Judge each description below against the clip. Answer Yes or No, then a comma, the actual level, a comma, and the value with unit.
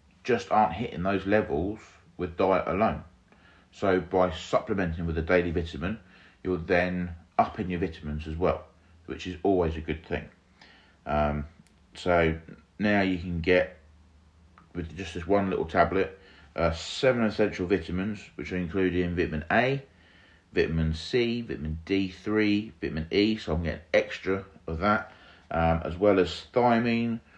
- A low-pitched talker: Yes, very low, 90 Hz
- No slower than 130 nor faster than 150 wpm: Yes, average, 145 wpm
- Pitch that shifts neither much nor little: Yes, average, 3.1 semitones